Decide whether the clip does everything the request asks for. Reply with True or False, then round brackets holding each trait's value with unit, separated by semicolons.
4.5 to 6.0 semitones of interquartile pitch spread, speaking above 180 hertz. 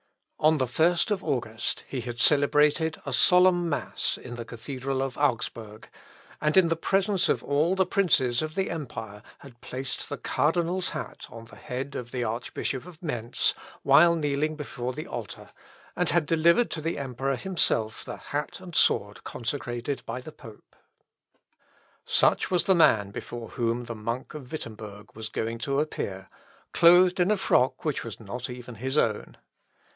False (5.6 semitones; 135 Hz)